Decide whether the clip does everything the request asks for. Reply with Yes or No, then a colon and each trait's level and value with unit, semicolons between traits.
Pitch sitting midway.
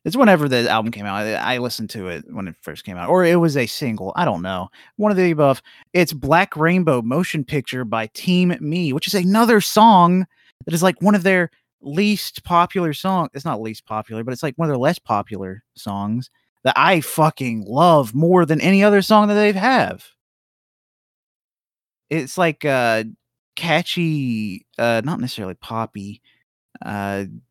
Yes: medium, 155 Hz